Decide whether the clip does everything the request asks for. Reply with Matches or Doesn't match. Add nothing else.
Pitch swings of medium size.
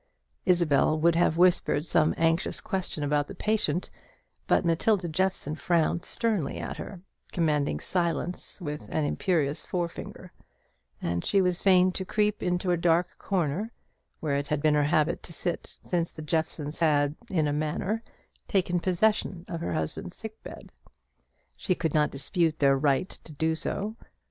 Matches